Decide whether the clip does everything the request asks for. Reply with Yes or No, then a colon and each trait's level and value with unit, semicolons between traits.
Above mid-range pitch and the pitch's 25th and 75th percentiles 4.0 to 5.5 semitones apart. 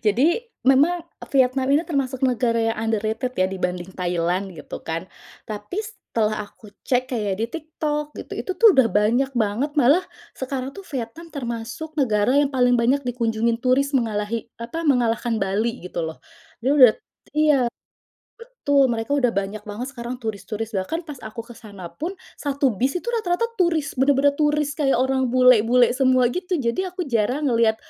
Yes: very high, 250 Hz; average, 4.5 semitones